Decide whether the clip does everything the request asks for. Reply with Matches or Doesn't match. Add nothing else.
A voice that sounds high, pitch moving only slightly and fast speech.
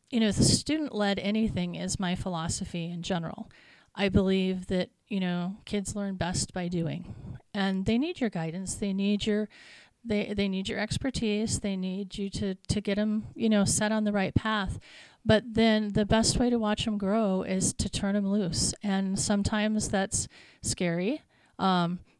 Doesn't match